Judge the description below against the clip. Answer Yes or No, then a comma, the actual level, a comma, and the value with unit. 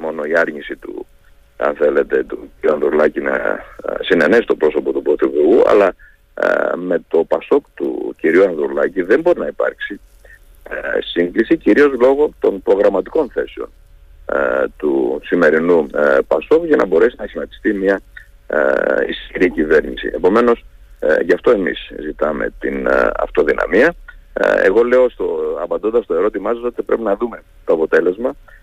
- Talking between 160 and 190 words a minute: No, average, 130 wpm